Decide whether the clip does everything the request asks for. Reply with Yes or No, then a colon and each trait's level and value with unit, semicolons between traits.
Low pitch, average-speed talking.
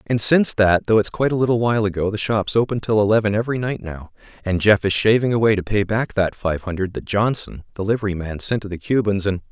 No: low, 105 Hz; fast, 245 wpm